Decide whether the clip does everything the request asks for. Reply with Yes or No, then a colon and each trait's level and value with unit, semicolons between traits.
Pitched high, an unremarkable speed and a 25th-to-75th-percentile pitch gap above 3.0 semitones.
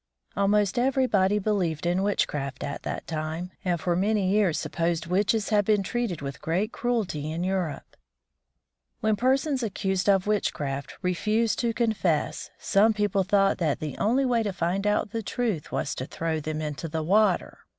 Yes: high, 195 Hz; average, 165 wpm; average, 4.5 semitones